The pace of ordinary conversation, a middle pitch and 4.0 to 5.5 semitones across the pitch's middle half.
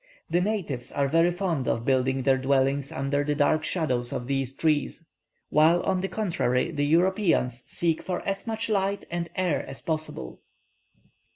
Yes: average, 165 wpm; medium, 155 Hz; average, 4.9 semitones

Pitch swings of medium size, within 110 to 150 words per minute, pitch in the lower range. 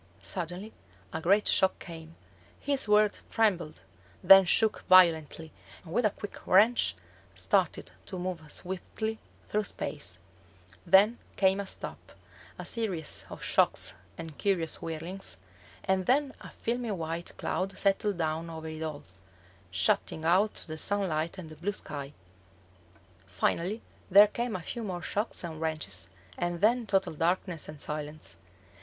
No: average, 4.3 semitones; average, 140 wpm; medium, 180 Hz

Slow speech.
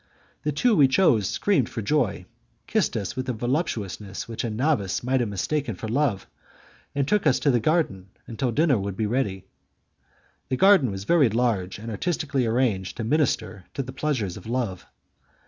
No: average, 180 wpm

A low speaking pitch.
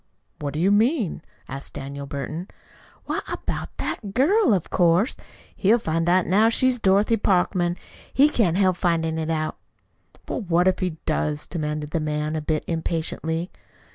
No: medium, 175 Hz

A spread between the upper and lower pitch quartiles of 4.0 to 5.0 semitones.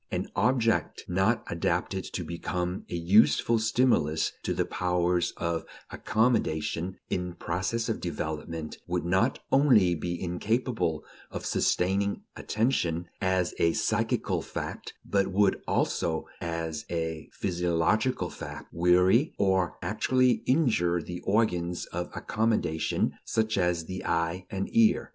Yes: average, 4.3 semitones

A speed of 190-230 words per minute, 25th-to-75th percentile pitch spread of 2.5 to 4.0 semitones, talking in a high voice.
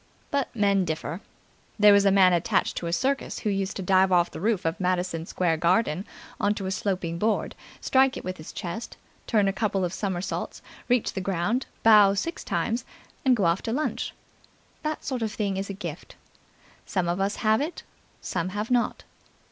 Yes: average, 195 wpm; average, 3.5 semitones; high, 195 Hz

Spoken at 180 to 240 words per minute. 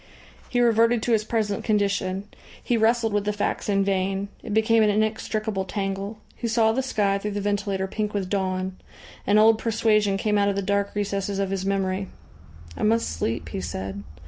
Yes: average, 190 wpm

